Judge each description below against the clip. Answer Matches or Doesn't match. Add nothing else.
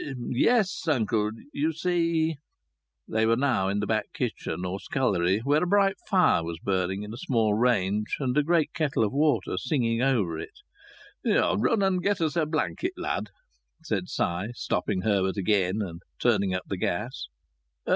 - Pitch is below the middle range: Matches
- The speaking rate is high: Doesn't match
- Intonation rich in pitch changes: Matches